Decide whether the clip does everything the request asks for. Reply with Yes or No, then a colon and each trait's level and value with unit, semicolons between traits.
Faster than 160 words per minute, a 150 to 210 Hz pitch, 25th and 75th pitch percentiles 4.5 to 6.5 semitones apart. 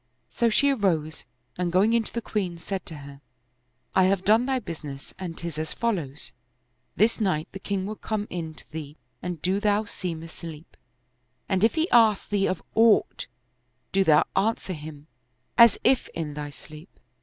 Yes: average, 180 wpm; medium, 185 Hz; average, 5.2 semitones